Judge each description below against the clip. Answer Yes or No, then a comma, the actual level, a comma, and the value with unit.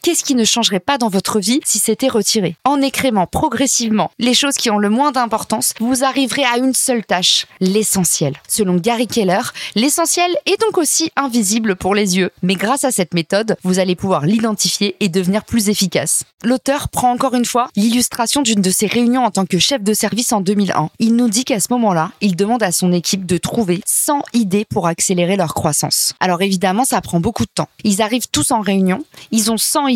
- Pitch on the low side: No, high, 220 Hz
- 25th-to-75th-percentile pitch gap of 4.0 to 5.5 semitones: Yes, average, 4.7 semitones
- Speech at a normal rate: Yes, average, 210 wpm